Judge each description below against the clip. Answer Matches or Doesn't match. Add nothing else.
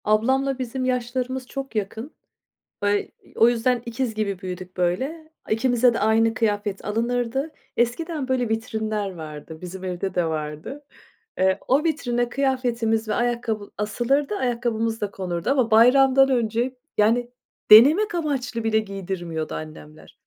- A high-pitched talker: Matches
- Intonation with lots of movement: Doesn't match